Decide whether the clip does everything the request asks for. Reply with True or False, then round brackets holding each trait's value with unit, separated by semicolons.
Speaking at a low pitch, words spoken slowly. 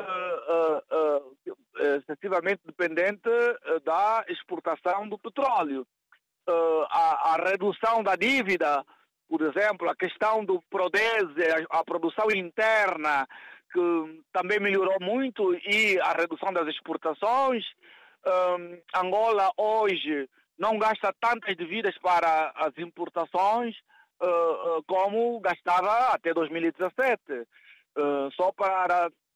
False (185 Hz; 110 wpm)